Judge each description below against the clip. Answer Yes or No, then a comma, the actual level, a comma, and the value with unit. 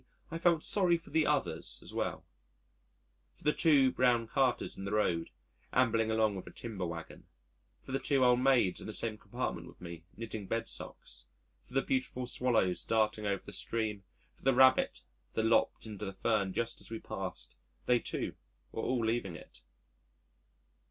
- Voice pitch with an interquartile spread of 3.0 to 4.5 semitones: Yes, average, 4.1 semitones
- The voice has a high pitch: No, low, 115 Hz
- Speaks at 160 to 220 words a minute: Yes, average, 180 wpm